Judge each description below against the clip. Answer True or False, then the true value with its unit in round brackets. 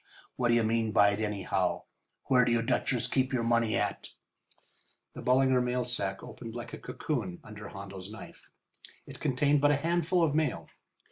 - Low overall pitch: True (120 Hz)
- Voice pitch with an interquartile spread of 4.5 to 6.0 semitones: False (3.7 semitones)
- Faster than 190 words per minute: False (175 wpm)